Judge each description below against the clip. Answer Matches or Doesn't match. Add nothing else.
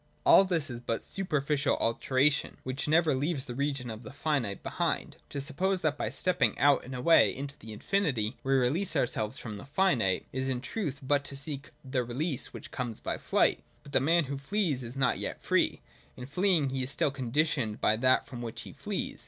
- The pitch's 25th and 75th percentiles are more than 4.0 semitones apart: Doesn't match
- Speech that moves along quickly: Matches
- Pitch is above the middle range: Doesn't match